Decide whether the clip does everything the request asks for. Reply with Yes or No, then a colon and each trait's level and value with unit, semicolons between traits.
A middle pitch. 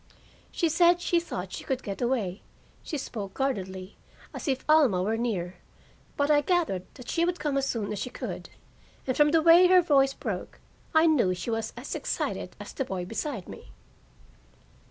No: very high, 265 Hz